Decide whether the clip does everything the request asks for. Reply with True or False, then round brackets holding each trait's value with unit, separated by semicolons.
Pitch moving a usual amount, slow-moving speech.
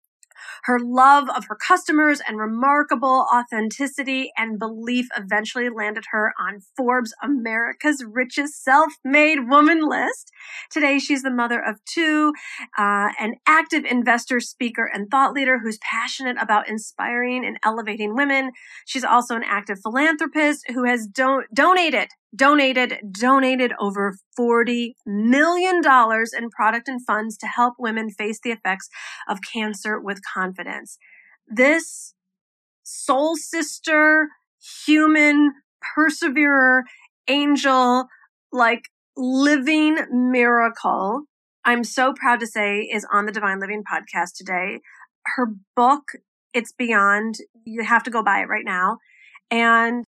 True (4.5 semitones; 125 wpm)